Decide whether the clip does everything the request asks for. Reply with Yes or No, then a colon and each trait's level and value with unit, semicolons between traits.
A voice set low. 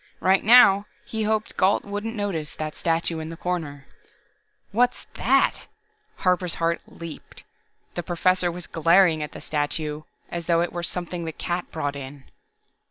No: medium, 170 Hz